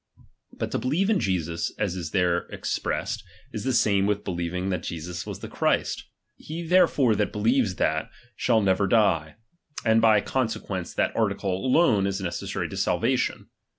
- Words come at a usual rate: Yes, average, 165 wpm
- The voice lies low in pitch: Yes, low, 100 Hz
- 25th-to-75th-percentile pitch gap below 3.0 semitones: No, average, 4.3 semitones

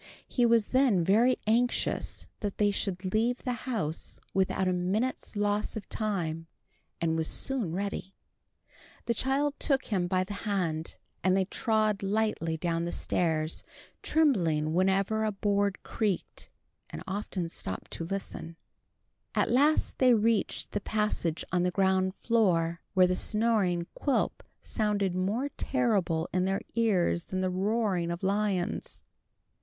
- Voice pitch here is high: Yes, high, 195 Hz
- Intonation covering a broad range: No, average, 3.7 semitones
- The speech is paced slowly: No, average, 145 wpm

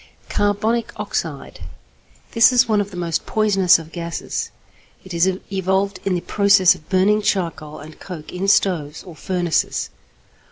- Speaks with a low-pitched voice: No, high, 190 Hz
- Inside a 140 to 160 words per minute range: Yes, average, 150 wpm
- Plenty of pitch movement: No, average, 3.2 semitones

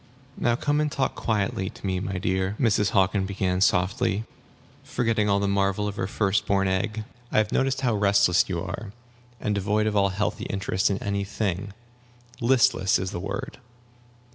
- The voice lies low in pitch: Yes, low, 100 Hz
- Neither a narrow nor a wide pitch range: No, narrow, 2.1 semitones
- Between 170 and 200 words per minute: Yes, average, 180 wpm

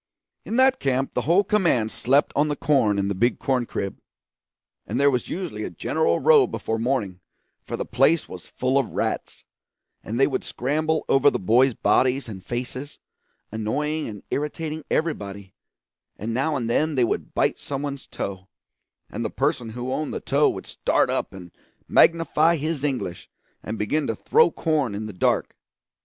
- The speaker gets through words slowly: No, average, 175 wpm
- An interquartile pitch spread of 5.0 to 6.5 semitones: Yes, wide, 5.5 semitones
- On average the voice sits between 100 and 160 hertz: Yes, low, 135 Hz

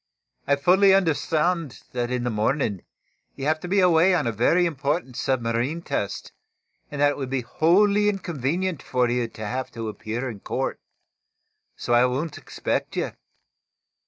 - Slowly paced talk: No, average, 160 wpm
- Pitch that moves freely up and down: Yes, wide, 5.9 semitones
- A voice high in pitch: No, medium, 140 Hz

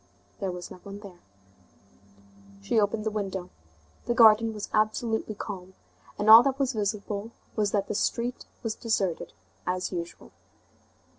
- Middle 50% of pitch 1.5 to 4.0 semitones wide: Yes, narrow, 2.6 semitones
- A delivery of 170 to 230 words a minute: No, average, 145 wpm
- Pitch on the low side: No, high, 210 Hz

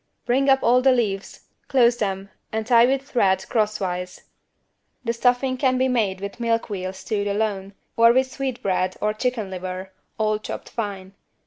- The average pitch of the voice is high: Yes, high, 220 Hz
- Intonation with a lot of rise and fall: No, average, 4.3 semitones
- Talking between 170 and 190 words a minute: No, average, 160 wpm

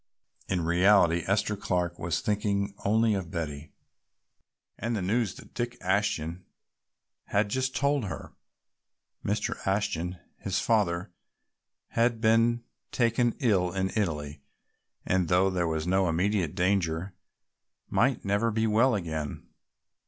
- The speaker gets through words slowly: Yes, slow, 125 wpm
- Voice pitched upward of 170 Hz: No, very low, 95 Hz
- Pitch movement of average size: Yes, average, 4.2 semitones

